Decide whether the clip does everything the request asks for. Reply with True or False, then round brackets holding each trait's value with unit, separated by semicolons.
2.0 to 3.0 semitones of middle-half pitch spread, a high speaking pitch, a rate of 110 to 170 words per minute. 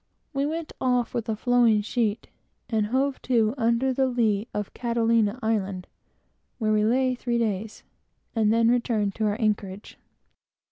True (2.5 semitones; 230 Hz; 150 wpm)